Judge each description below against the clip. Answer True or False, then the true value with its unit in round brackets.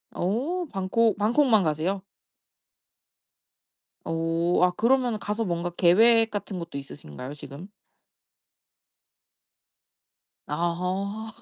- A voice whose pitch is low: False (190 Hz)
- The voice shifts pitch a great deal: False (4.8 semitones)